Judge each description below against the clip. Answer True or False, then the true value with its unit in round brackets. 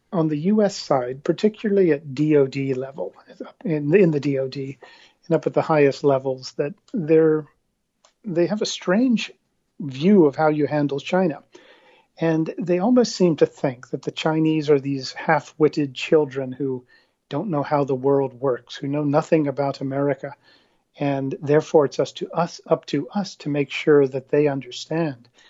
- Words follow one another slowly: False (165 wpm)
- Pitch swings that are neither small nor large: True (3.5 semitones)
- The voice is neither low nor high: True (150 Hz)